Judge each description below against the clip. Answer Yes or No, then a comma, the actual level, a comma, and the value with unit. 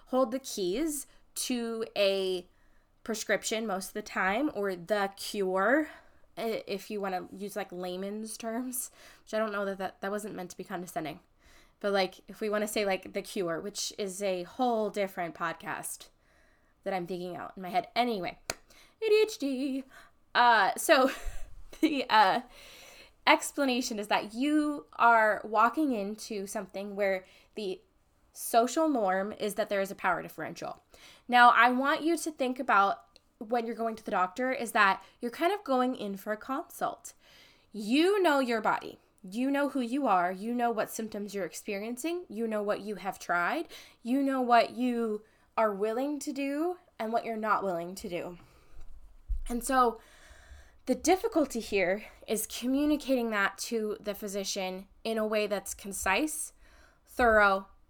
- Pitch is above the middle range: Yes, high, 220 Hz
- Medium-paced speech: Yes, average, 165 wpm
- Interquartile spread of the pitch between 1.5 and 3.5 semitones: No, average, 4.8 semitones